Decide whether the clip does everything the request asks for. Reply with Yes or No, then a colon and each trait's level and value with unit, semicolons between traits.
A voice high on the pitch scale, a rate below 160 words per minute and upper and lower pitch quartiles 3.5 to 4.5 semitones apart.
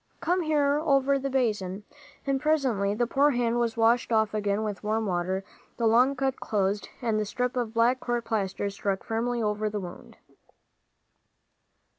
No: high, 230 Hz; average, 165 wpm; average, 3.9 semitones